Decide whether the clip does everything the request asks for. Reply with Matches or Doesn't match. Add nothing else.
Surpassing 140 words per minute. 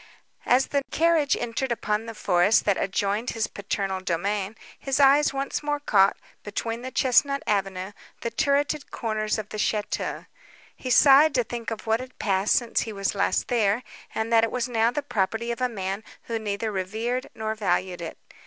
Matches